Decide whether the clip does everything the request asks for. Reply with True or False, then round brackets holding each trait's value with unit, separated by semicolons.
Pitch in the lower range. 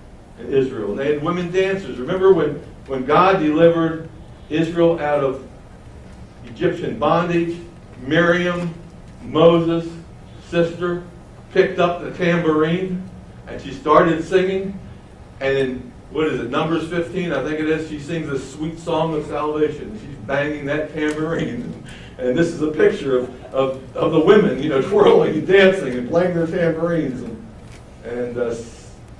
False (160 Hz)